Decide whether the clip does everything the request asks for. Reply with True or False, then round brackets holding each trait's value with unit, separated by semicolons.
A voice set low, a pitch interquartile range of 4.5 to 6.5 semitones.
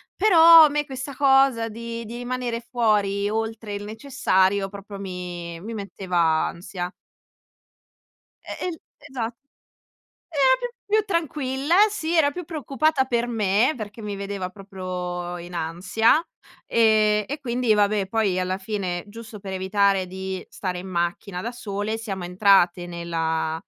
False (210 Hz; 5.1 semitones)